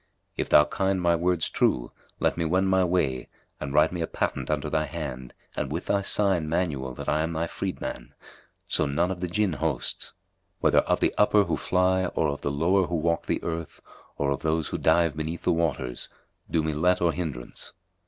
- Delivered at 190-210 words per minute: Yes, fast, 205 wpm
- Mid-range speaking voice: No, very low, 80 Hz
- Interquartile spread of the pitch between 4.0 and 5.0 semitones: No, average, 3.2 semitones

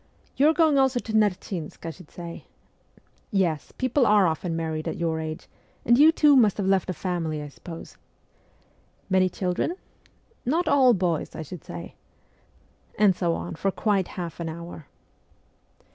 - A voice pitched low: No, medium, 185 Hz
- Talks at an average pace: Yes, average, 165 wpm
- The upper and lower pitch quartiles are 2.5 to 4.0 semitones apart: No, average, 5.2 semitones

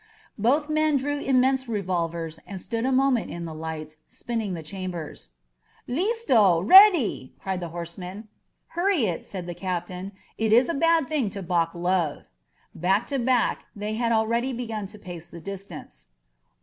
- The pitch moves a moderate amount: No, wide, 6.7 semitones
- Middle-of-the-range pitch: No, high, 205 Hz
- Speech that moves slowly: No, average, 165 wpm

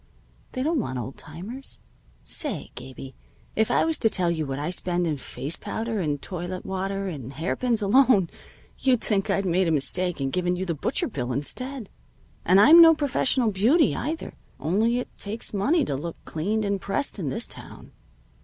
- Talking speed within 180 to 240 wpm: Yes, average, 185 wpm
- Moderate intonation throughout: No, wide, 6.6 semitones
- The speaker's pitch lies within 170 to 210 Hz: Yes, high, 190 Hz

